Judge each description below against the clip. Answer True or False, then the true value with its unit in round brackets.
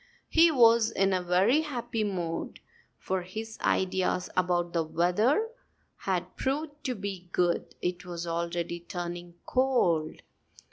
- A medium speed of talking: False (130 wpm)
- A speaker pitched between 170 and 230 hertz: True (185 Hz)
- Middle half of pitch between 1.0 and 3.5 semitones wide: False (5.0 semitones)